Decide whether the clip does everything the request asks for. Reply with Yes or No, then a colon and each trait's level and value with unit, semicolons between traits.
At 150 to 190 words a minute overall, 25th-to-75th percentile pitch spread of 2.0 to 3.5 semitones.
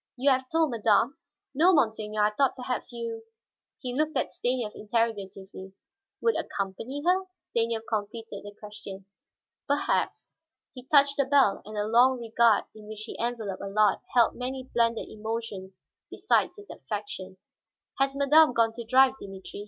No: average, 155 wpm; average, 3.9 semitones